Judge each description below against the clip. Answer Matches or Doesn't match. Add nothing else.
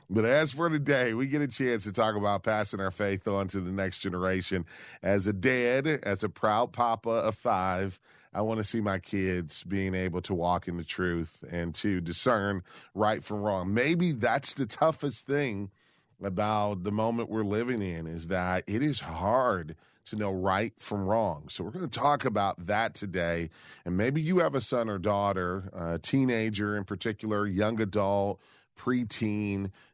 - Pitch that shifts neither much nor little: Matches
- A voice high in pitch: Doesn't match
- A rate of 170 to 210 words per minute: Matches